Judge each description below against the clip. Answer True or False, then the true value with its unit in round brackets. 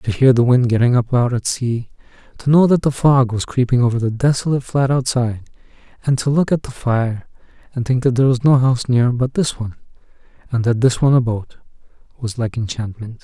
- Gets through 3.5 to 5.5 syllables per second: False (5.8 syllables/s)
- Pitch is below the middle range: True (125 Hz)